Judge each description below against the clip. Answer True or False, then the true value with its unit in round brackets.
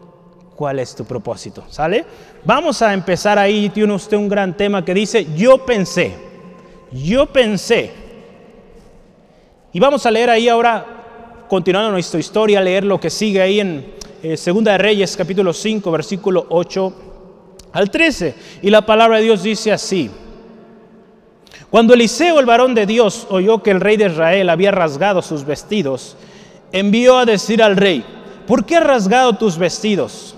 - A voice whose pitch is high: True (205 Hz)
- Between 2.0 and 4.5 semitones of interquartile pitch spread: True (3.0 semitones)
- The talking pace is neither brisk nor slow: True (160 wpm)